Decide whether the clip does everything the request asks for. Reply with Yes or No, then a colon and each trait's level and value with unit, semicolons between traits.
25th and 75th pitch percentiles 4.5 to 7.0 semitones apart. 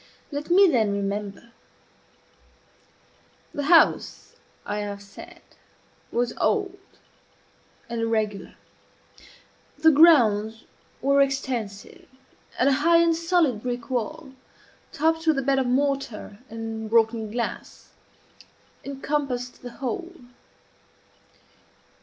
Yes: average, 5.2 semitones